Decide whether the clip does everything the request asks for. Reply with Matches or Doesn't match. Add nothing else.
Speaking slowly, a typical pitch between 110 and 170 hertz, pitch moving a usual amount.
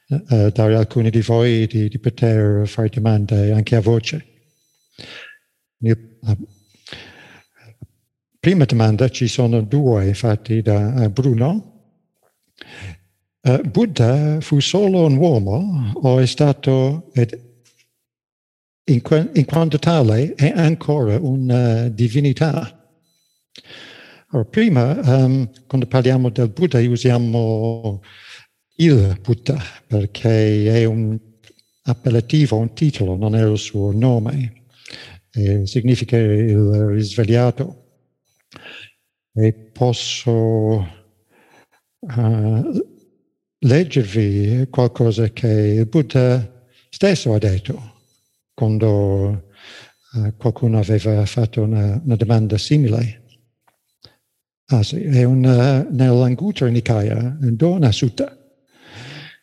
Matches